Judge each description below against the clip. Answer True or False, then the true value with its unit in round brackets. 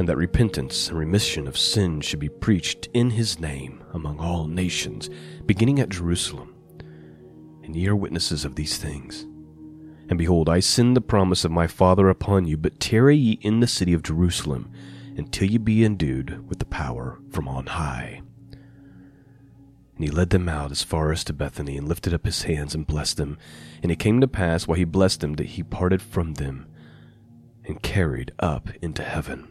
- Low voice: True (85 Hz)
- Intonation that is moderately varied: True (4.8 semitones)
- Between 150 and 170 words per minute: False (185 wpm)